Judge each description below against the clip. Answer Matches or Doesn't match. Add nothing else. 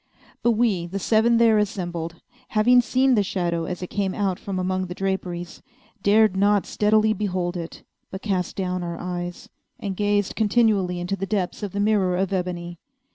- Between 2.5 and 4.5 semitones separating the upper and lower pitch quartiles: Matches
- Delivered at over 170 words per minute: Matches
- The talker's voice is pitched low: Doesn't match